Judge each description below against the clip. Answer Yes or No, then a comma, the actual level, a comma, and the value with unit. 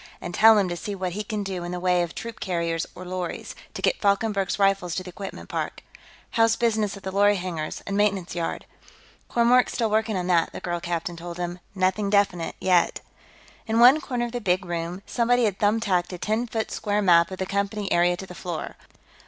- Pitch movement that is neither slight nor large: Yes, average, 3.3 semitones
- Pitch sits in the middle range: No, high, 195 Hz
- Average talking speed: No, fast, 215 wpm